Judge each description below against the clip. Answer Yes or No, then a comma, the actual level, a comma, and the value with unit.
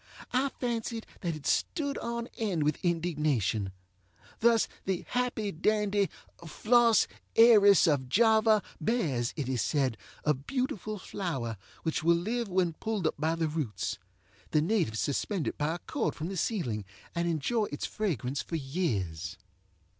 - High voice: No, medium, 175 Hz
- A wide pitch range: Yes, wide, 7.0 semitones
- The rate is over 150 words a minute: No, average, 145 wpm